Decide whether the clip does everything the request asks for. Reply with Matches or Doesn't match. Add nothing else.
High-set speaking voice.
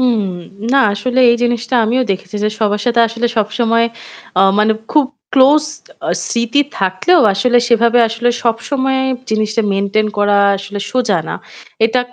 Matches